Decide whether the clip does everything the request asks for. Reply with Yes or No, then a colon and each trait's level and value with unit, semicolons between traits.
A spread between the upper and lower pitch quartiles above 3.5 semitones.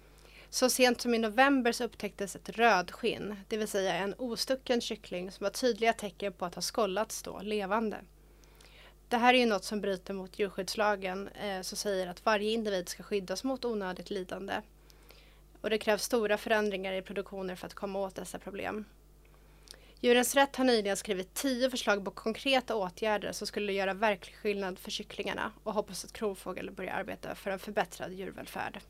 No: average, 2.9 semitones